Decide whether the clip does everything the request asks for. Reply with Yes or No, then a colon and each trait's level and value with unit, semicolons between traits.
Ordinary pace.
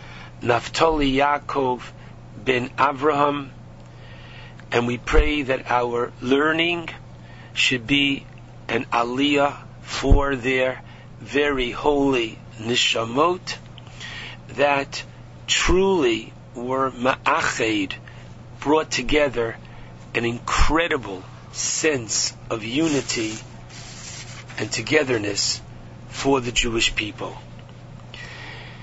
No: slow, 75 wpm